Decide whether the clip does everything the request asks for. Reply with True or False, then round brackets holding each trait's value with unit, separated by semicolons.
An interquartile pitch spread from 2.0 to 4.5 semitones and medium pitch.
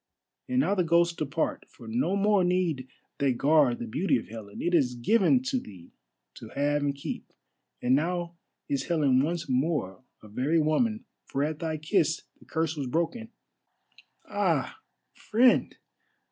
False (4.9 semitones; 155 Hz)